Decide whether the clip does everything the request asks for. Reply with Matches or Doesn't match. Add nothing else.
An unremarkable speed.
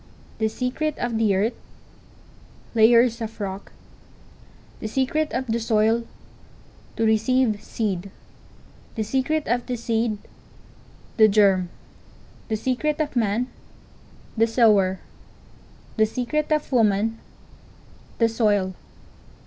Doesn't match